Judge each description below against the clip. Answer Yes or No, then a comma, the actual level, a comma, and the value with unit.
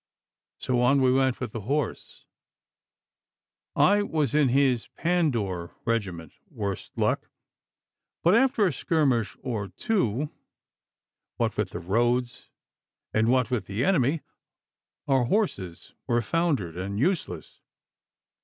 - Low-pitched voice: Yes, low, 125 Hz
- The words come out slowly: Yes, slow, 115 wpm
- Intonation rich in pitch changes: Yes, wide, 6.4 semitones